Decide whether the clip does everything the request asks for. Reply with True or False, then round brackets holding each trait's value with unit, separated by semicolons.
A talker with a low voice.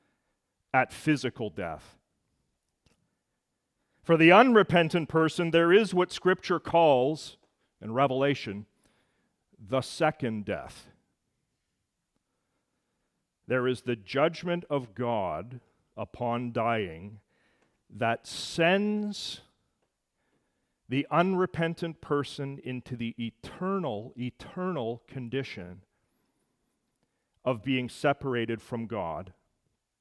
True (130 Hz)